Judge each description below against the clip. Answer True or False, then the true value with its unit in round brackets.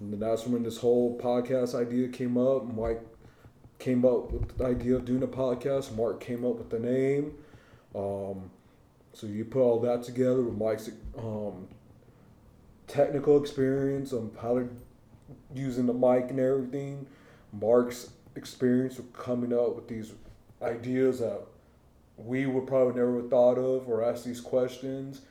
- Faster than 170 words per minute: False (155 wpm)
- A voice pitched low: True (125 Hz)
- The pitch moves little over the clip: True (2.1 semitones)